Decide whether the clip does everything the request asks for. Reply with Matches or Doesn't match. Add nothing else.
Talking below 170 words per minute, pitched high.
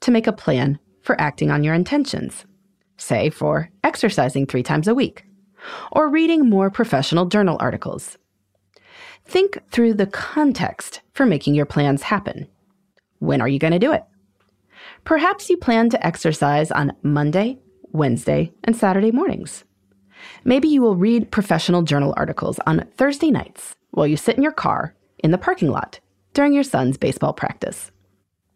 Matches